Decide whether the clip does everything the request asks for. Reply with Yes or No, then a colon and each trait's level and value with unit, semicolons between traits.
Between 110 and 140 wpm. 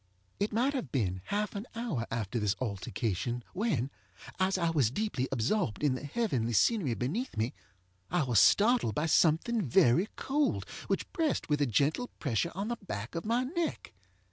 No: average, 170 wpm